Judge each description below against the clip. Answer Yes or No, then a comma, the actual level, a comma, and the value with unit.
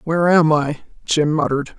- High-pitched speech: No, medium, 155 Hz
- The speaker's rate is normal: Yes, average, 170 wpm